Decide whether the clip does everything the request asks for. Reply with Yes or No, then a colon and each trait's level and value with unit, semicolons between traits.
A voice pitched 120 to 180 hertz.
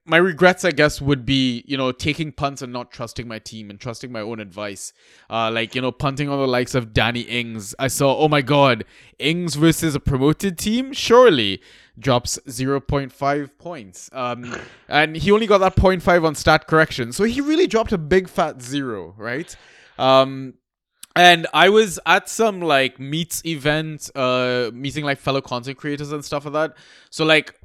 Yes: medium, 140 Hz